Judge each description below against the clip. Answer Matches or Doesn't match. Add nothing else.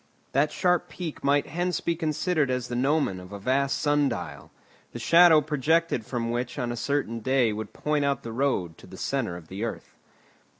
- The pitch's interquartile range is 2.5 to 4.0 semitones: Doesn't match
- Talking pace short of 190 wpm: Doesn't match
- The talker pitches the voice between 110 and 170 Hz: Matches